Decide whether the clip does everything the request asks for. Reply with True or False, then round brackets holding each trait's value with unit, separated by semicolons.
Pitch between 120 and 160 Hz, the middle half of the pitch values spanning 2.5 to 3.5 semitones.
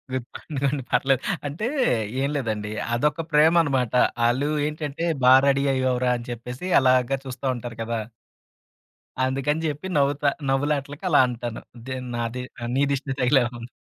True (135 Hz; 2.8 semitones)